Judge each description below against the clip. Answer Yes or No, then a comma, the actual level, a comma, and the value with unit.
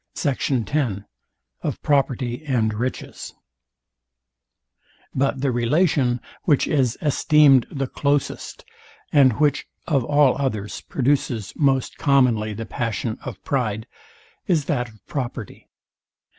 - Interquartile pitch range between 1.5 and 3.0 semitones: No, average, 3.4 semitones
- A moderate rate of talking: No, slow, 115 wpm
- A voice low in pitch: Yes, low, 130 Hz